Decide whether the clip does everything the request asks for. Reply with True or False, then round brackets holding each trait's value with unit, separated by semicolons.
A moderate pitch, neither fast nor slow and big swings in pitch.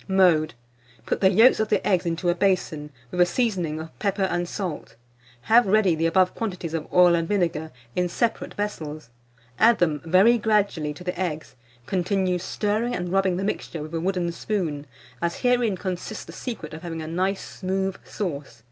False (180 Hz; 185 wpm; 3.5 semitones)